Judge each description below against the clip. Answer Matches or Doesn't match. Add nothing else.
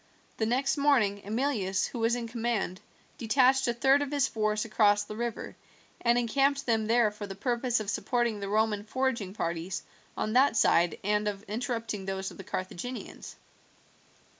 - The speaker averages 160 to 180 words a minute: Matches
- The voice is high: Matches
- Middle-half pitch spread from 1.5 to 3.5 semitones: Matches